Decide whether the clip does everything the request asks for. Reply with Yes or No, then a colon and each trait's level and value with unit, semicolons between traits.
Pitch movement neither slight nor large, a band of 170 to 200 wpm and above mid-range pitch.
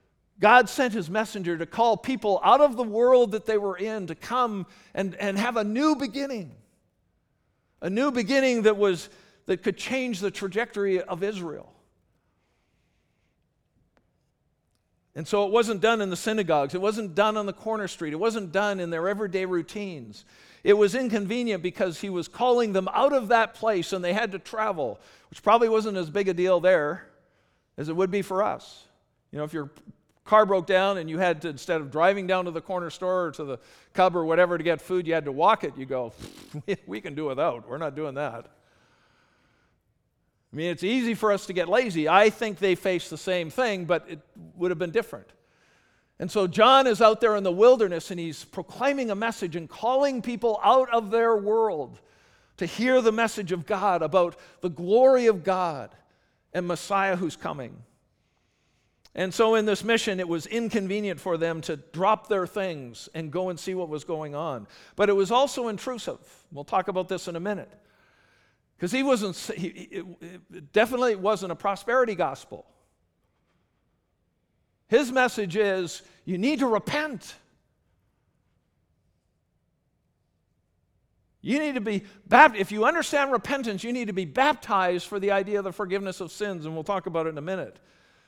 Yes: average, 4.7 semitones; average, 185 wpm; high, 195 Hz